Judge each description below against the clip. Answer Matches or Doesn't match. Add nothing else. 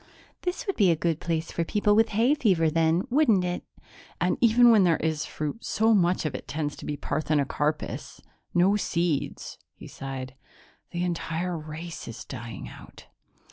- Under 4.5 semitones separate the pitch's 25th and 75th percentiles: Doesn't match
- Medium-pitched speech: Matches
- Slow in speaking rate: Doesn't match